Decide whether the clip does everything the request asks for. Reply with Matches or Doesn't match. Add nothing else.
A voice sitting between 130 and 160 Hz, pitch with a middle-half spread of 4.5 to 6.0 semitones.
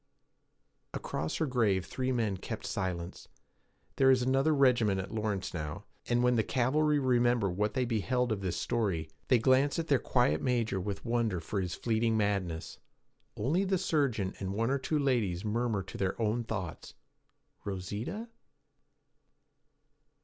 Doesn't match